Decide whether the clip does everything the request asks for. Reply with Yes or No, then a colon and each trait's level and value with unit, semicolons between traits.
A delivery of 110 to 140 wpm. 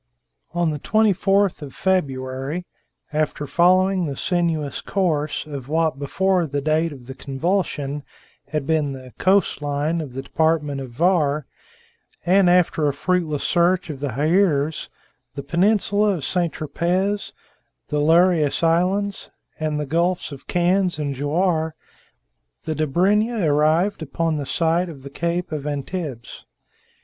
Yes: slow, 135 wpm